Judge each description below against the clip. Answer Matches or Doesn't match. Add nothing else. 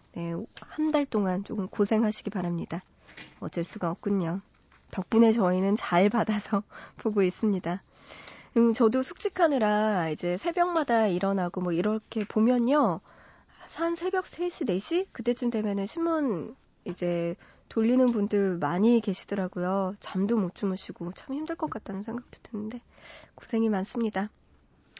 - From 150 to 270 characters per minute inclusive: Doesn't match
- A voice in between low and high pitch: Doesn't match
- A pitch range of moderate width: Matches